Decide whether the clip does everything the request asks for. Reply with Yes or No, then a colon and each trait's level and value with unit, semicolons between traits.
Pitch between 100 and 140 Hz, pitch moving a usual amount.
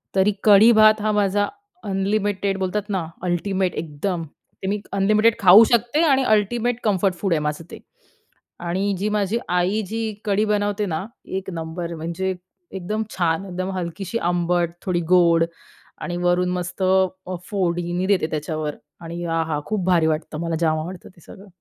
No: medium, 185 Hz; average, 3.2 semitones